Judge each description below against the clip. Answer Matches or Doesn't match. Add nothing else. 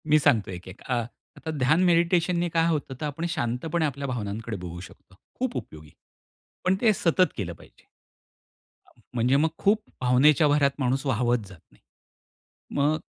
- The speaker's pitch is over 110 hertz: Matches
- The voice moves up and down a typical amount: Doesn't match